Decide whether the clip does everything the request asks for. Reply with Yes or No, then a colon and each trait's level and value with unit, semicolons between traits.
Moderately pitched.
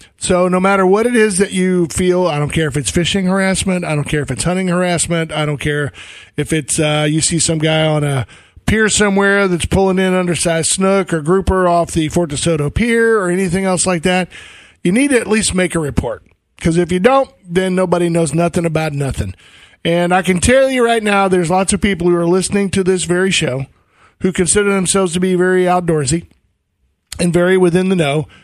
Yes: medium, 180 Hz